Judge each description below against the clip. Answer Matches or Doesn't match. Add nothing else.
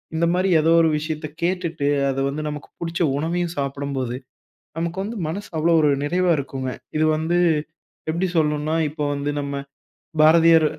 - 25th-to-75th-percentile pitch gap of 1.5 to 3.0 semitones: Matches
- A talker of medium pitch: Matches